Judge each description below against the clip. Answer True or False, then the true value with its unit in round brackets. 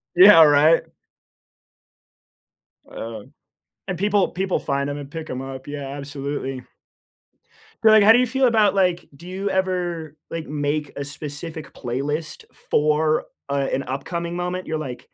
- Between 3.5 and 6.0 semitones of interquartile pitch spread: True (4.4 semitones)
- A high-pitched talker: False (155 Hz)